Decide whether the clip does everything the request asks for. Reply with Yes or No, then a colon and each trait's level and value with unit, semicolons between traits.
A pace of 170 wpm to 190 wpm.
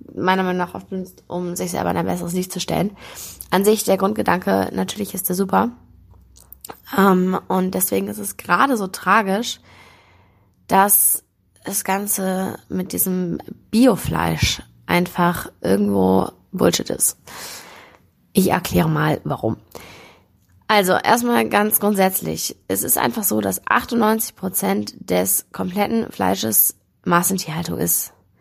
No: slow, 125 wpm